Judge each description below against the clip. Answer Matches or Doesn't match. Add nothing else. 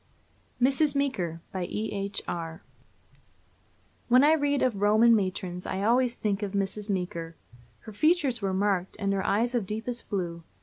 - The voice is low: Doesn't match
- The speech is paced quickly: Doesn't match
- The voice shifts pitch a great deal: Doesn't match